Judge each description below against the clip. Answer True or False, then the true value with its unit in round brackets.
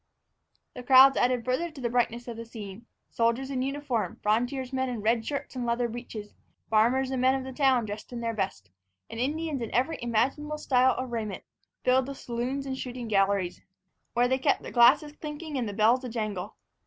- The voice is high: True (245 Hz)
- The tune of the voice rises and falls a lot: False (2.5 semitones)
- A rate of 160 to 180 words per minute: False (195 wpm)